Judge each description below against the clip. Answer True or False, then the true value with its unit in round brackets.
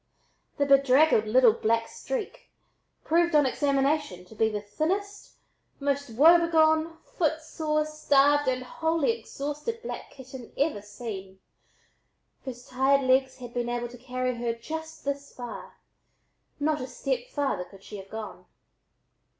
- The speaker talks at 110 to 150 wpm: True (135 wpm)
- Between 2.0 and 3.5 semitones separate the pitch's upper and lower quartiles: False (4.4 semitones)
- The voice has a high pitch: True (275 Hz)